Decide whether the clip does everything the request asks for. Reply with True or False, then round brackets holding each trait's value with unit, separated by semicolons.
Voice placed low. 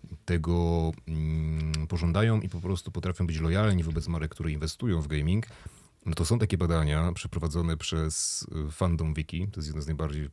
True (85 Hz)